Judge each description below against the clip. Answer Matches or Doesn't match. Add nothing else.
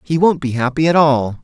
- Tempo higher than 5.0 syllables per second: Matches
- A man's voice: Matches